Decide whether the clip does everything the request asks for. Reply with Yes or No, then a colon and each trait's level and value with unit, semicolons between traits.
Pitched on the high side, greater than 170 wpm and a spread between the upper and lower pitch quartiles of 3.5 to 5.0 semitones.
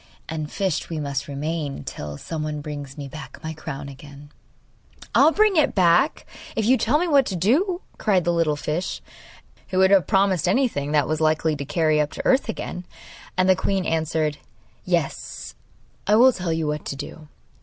No: medium, 160 Hz; average, 190 wpm; average, 4.6 semitones